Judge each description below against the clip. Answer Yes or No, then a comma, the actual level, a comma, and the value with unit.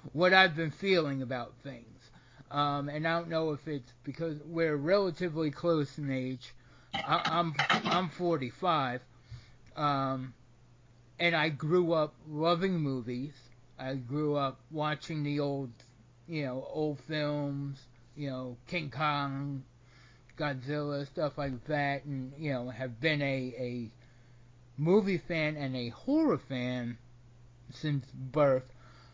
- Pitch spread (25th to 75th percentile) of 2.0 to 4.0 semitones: Yes, average, 3.6 semitones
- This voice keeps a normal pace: No, slow, 130 wpm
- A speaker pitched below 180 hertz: Yes, medium, 140 Hz